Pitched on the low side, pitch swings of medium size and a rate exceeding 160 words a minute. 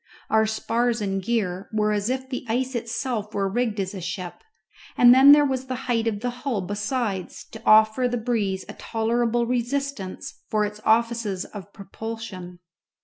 No: high, 225 Hz; average, 3.1 semitones; average, 175 wpm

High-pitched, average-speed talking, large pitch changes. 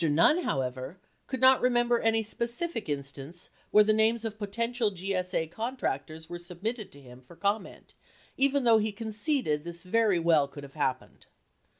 Yes: high, 200 Hz; average, 165 wpm; wide, 6.4 semitones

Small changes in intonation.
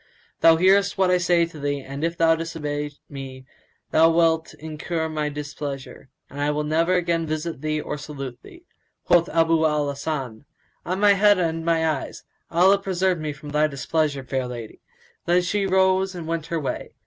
No: average, 3.0 semitones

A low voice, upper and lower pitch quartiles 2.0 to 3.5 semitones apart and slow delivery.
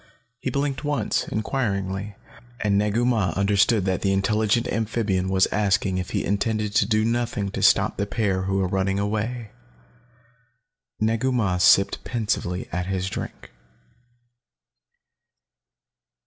Yes: low, 105 Hz; average, 2.7 semitones; slow, 130 wpm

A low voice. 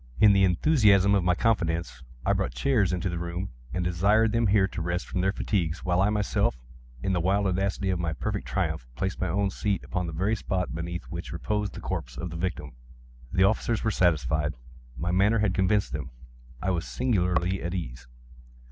Yes: very low, 95 Hz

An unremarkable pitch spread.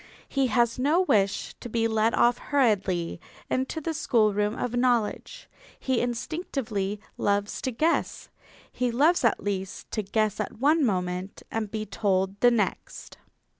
Yes: average, 4.2 semitones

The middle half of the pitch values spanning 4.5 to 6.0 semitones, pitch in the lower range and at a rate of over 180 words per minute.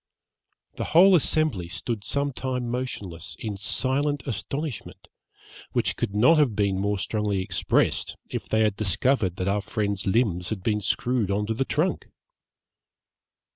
No: average, 4.9 semitones; low, 110 Hz; average, 145 wpm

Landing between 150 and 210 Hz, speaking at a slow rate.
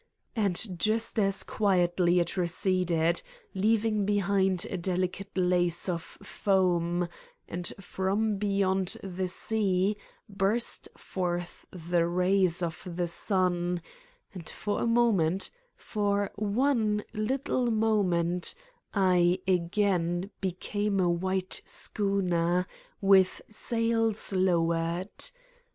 Yes: high, 190 Hz; slow, 100 wpm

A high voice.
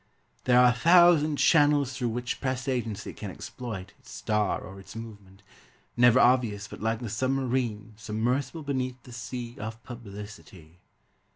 No: low, 120 Hz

